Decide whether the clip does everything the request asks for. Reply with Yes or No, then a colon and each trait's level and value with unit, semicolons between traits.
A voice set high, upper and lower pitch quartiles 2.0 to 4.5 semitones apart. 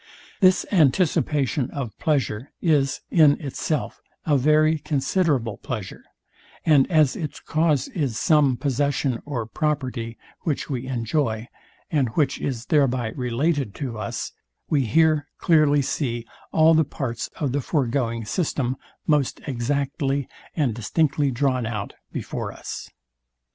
No: medium, 140 Hz; average, 3.9 semitones